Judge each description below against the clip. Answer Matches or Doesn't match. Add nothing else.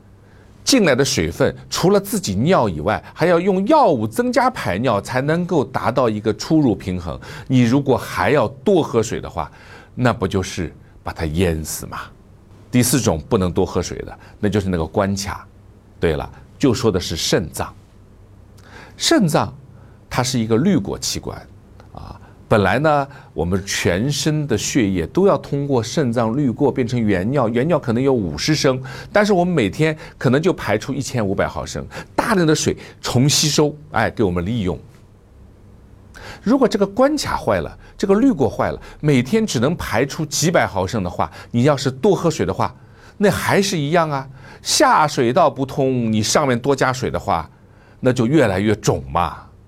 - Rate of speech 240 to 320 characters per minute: Matches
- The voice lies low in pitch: Matches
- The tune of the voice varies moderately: Doesn't match